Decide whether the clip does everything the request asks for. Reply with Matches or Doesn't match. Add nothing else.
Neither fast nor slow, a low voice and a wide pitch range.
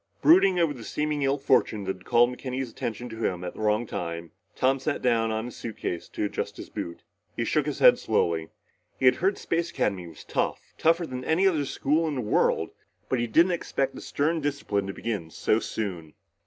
Doesn't match